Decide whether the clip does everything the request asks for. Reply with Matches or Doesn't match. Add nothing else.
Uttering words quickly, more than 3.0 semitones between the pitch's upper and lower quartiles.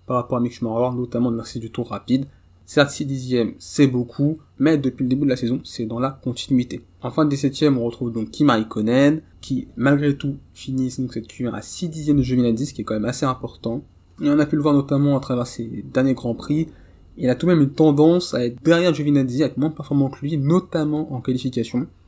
Matches